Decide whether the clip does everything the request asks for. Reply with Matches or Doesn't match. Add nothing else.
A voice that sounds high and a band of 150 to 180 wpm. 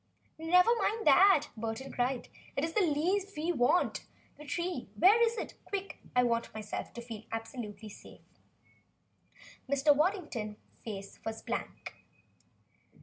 Doesn't match